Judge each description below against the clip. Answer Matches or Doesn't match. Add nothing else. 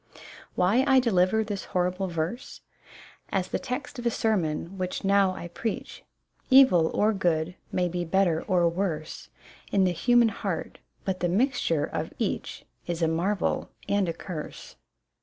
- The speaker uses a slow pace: Doesn't match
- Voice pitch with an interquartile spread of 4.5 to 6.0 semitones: Doesn't match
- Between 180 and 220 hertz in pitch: Matches